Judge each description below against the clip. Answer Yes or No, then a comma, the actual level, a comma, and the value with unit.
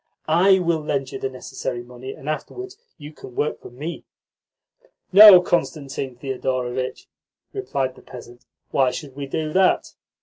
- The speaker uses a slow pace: No, average, 145 wpm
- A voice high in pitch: No, medium, 140 Hz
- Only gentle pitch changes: No, average, 4.3 semitones